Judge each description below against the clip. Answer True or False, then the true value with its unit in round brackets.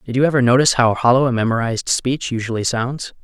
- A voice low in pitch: True (125 Hz)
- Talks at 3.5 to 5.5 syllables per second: False (6.6 syllables/s)